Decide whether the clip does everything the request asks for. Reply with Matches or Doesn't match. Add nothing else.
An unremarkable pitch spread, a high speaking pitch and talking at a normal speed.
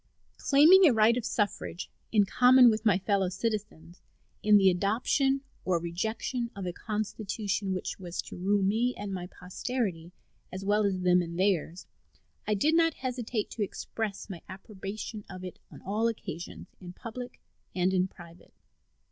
Matches